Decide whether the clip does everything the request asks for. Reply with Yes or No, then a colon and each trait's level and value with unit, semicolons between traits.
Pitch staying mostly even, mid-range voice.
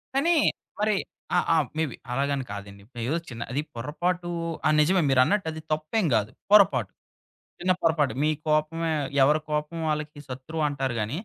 No: average, 3.8 semitones; medium, 150 Hz